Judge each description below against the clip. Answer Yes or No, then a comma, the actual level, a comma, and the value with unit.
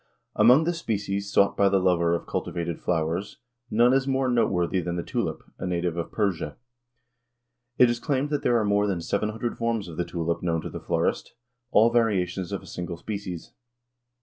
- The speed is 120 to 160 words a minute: No, average, 190 wpm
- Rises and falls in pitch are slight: No, average, 5.1 semitones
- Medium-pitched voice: No, low, 100 Hz